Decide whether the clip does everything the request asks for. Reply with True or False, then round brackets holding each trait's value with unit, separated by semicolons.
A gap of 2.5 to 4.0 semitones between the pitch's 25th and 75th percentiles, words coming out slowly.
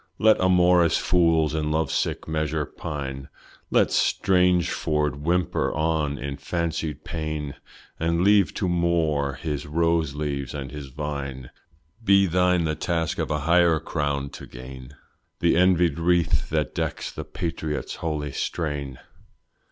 True (2.8 semitones; 130 wpm)